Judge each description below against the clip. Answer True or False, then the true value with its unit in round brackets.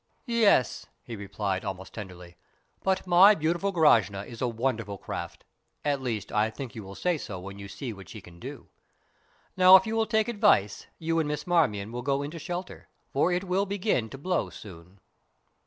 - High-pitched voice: False (135 Hz)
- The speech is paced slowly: False (190 wpm)